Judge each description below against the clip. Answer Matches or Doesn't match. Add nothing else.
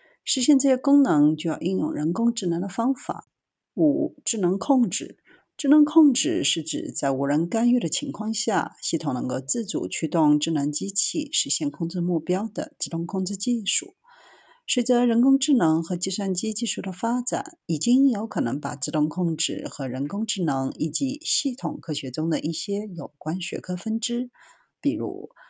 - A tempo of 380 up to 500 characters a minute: Doesn't match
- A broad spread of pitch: Matches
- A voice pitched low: Doesn't match